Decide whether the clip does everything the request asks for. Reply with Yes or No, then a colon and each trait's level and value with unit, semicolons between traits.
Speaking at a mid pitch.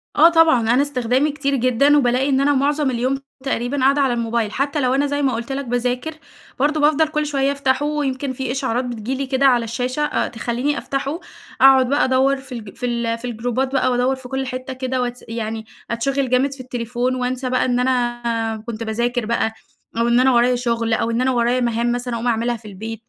No: very high, 255 Hz